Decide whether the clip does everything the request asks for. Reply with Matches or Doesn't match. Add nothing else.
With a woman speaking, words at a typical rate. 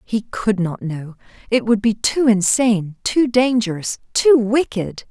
Matches